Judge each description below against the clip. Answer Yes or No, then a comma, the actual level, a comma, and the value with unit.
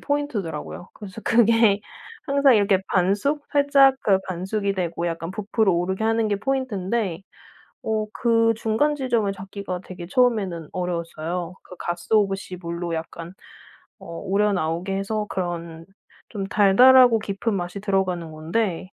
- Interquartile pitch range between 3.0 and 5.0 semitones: Yes, average, 4.2 semitones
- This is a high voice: Yes, high, 195 Hz